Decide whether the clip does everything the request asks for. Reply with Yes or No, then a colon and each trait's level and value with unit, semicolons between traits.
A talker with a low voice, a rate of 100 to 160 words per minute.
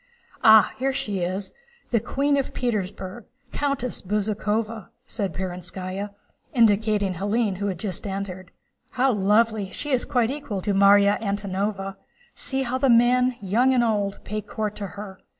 No: high, 210 Hz; average, 150 wpm